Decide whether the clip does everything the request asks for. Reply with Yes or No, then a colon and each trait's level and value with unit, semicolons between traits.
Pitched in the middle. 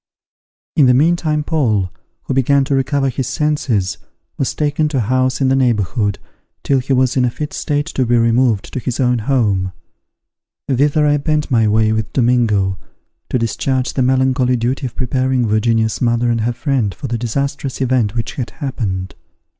No: low, 125 Hz